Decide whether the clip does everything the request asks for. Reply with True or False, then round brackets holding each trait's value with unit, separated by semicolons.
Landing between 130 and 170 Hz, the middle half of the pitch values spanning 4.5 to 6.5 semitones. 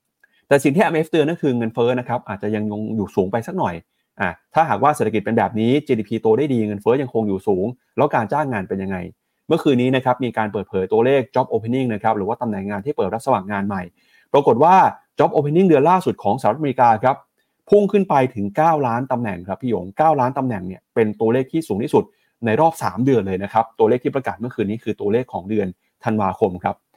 False (115 Hz; 5.2 semitones)